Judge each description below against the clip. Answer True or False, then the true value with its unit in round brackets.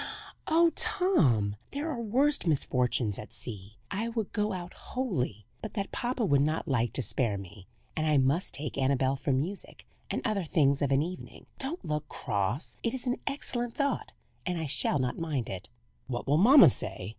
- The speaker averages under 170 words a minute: False (185 wpm)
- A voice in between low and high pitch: True (155 Hz)